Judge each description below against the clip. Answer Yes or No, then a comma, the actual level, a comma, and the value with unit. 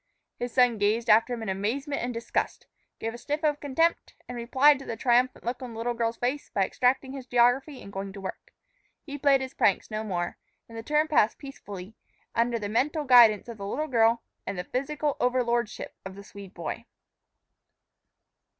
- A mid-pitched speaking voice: No, high, 240 Hz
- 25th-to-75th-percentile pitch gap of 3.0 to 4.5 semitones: Yes, average, 3.8 semitones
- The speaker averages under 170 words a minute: No, average, 195 wpm